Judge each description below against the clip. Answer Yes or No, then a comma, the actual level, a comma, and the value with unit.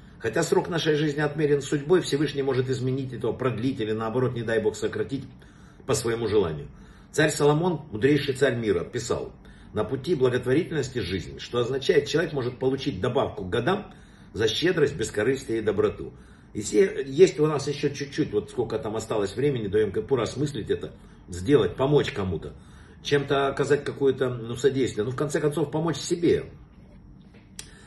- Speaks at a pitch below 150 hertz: Yes, medium, 140 Hz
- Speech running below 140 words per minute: No, fast, 160 wpm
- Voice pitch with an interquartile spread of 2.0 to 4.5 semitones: Yes, average, 3.1 semitones